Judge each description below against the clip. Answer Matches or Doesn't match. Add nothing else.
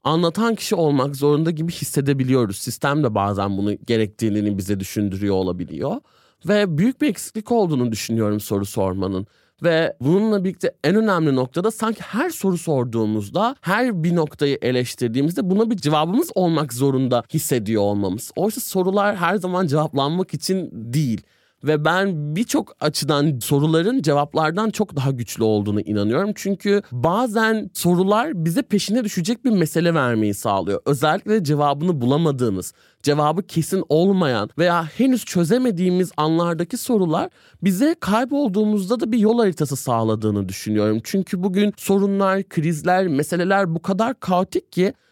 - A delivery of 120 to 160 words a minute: Matches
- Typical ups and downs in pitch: Doesn't match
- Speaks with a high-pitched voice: Doesn't match